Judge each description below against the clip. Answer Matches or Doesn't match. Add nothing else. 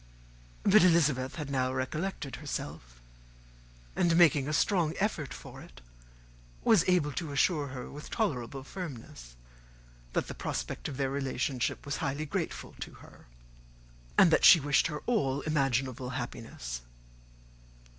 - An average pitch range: Matches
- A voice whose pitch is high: Doesn't match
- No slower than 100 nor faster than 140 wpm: Matches